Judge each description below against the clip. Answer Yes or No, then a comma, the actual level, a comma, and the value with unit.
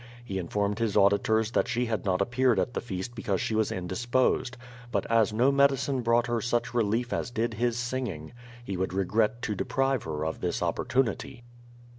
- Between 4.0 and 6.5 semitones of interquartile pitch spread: No, average, 3.5 semitones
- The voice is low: Yes, low, 115 Hz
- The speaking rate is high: No, average, 185 wpm